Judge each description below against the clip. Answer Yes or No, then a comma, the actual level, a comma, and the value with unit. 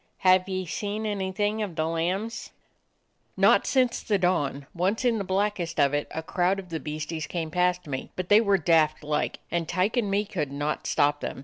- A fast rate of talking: Yes, fast, 210 wpm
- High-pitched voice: No, medium, 180 Hz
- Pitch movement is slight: No, average, 4.2 semitones